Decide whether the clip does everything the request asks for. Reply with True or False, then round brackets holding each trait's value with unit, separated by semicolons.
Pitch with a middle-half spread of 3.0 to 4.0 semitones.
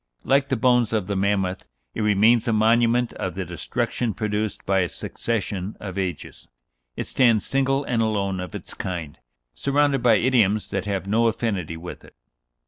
True (3.7 semitones)